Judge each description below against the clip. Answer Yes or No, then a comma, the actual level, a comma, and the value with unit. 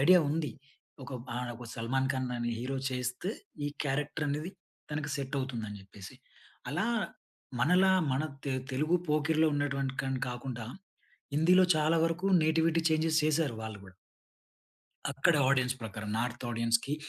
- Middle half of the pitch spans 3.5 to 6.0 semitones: Yes, average, 4.1 semitones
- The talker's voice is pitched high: No, medium, 140 Hz